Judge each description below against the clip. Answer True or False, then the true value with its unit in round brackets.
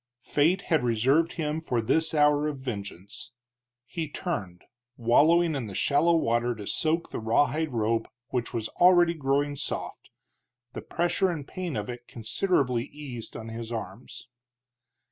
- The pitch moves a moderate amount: False (5.8 semitones)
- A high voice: False (135 Hz)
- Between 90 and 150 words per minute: True (145 wpm)